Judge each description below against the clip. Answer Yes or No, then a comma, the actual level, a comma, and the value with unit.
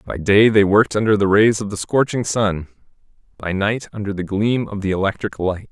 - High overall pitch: No, low, 105 Hz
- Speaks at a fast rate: Yes, fast, 210 wpm